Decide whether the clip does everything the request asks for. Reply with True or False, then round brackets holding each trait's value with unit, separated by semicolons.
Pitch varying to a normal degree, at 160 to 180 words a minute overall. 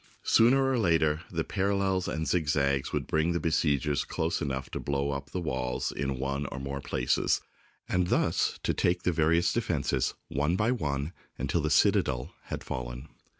True (4.3 semitones; 170 wpm)